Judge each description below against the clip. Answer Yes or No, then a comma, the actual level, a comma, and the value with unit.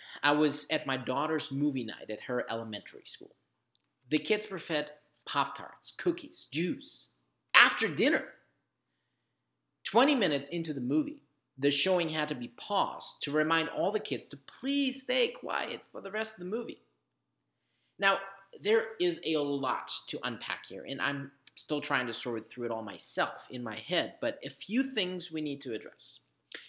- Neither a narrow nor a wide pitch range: No, wide, 7.3 semitones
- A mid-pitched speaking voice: Yes, medium, 150 Hz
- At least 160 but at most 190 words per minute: Yes, average, 170 wpm